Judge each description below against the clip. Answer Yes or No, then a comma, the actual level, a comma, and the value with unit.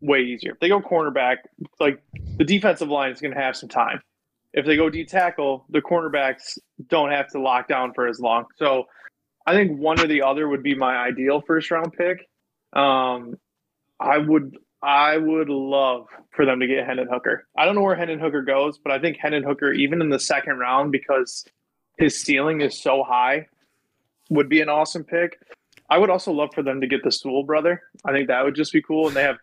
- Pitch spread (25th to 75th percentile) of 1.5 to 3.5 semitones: Yes, average, 2.9 semitones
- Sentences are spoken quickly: Yes, fast, 215 wpm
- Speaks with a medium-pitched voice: Yes, medium, 145 Hz